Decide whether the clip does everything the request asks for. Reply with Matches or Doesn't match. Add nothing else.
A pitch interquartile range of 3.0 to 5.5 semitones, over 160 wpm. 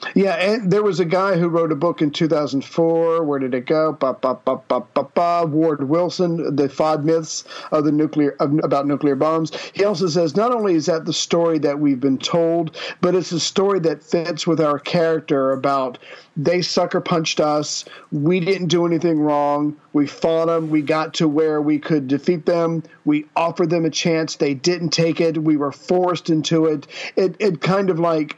Doesn't match